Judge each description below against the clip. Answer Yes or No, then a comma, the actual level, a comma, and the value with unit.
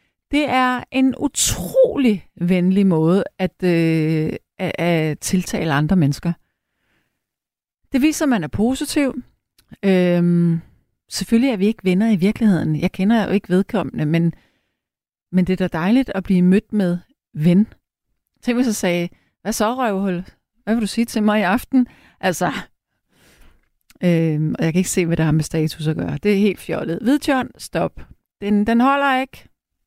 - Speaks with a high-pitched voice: Yes, high, 195 Hz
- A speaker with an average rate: Yes, average, 165 wpm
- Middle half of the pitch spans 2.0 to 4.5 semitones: No, average, 5.3 semitones